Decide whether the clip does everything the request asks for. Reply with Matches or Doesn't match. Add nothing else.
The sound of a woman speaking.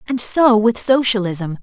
Matches